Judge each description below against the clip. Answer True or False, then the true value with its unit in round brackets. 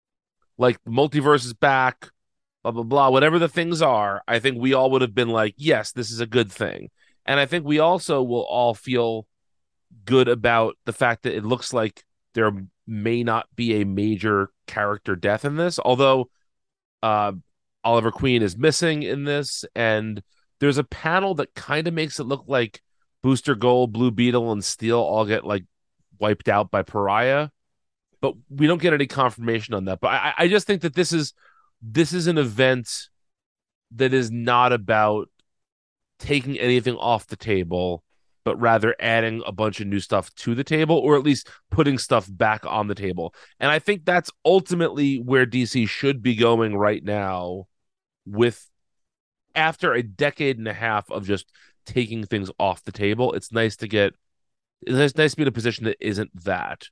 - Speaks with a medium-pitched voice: False (120 Hz)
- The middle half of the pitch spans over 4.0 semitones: True (4.5 semitones)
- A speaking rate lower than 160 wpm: False (180 wpm)